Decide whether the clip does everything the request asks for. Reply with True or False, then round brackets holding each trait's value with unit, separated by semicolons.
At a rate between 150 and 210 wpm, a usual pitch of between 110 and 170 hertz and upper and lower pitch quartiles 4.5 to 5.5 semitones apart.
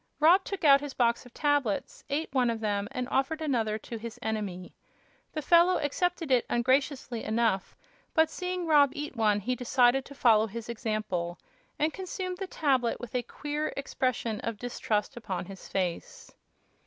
False (165 wpm; 250 Hz; 5.1 semitones)